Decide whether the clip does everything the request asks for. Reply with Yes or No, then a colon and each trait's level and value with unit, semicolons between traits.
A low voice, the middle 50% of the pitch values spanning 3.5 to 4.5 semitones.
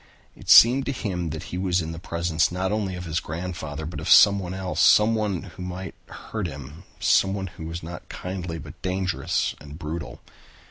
No: very low, 90 Hz; narrow, 2.6 semitones